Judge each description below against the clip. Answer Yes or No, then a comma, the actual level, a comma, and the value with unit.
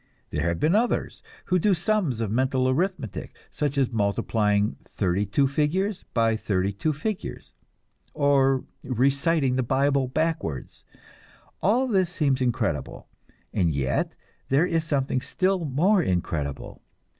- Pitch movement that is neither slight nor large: No, wide, 6.9 semitones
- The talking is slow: Yes, slow, 130 wpm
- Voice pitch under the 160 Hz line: Yes, low, 135 Hz